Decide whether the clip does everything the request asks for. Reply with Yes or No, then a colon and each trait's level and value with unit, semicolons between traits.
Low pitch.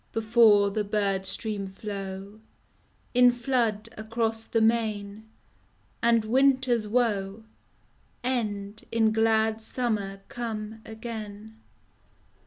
No: high, 220 Hz